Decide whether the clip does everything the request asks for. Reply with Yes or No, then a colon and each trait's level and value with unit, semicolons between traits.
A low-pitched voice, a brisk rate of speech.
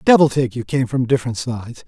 Yes: low, 125 Hz; fast, 225 wpm